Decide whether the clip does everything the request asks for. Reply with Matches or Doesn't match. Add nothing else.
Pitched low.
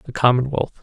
Matches